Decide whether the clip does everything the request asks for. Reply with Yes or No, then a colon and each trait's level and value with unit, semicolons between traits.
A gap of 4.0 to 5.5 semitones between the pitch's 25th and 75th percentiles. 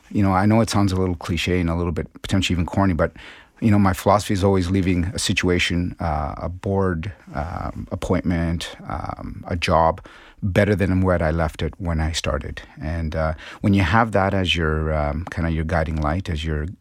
No: average, 3.2 semitones